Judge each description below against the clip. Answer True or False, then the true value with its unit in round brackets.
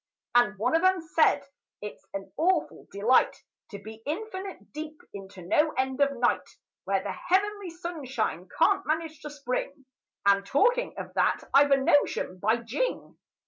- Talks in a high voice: True (285 Hz)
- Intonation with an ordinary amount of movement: False (6.7 semitones)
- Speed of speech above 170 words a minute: False (155 wpm)